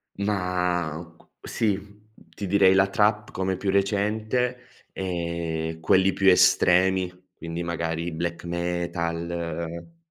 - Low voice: Yes, very low, 90 Hz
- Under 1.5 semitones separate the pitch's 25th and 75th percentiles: No, average, 2.7 semitones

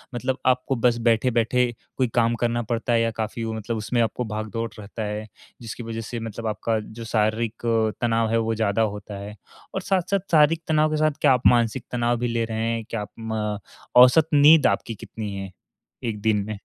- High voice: No, low, 115 Hz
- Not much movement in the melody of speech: Yes, narrow, 1.9 semitones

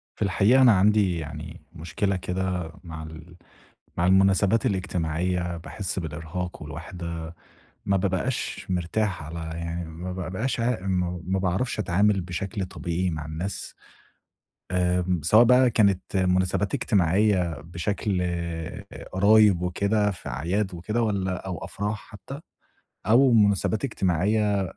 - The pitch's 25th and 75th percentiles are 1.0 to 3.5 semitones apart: Yes, average, 3.0 semitones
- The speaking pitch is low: Yes, very low, 95 Hz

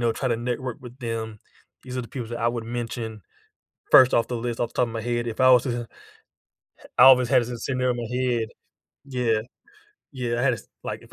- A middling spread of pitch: No, narrow, 1.6 semitones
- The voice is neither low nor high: No, low, 120 Hz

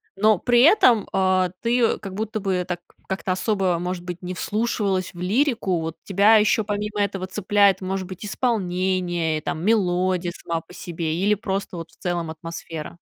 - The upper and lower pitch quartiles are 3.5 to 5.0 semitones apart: No, average, 2.9 semitones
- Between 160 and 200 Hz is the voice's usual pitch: Yes, medium, 185 Hz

